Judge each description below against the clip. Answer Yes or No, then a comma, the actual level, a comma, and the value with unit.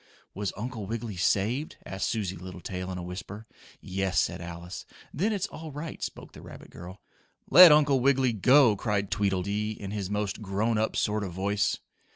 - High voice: No, low, 105 Hz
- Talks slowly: No, average, 175 wpm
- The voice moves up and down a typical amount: Yes, average, 4.1 semitones